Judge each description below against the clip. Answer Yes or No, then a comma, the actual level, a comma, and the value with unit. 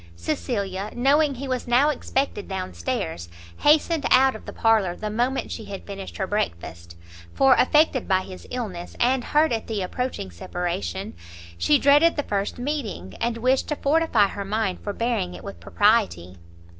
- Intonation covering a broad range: Yes, wide, 6.0 semitones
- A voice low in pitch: No, high, 220 Hz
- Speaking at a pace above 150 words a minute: Yes, average, 170 wpm